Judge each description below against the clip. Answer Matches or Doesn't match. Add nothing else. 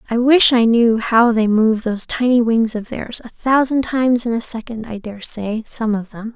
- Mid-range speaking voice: Doesn't match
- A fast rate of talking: Matches